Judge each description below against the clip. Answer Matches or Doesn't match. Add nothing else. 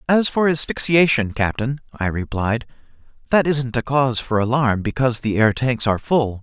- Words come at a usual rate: Matches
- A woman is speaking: Doesn't match